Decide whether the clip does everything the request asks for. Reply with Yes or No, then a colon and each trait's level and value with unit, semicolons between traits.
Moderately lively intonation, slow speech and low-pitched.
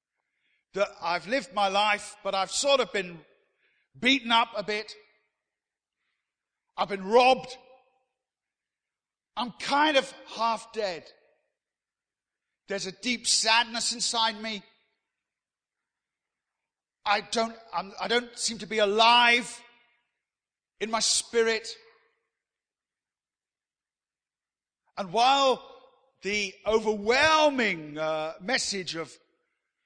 No: average, 3.9 semitones; slow, 95 wpm; high, 225 Hz